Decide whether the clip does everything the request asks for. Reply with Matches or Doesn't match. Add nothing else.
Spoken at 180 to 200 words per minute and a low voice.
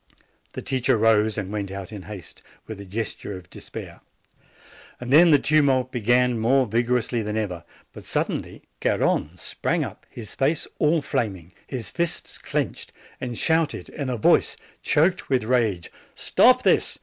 Doesn't match